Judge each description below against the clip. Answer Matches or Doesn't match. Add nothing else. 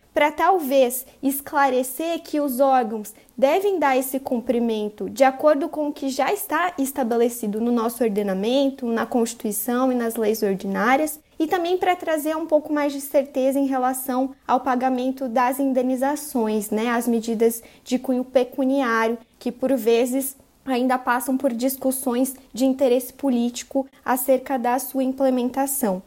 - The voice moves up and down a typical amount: Doesn't match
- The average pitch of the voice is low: Doesn't match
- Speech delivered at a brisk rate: Doesn't match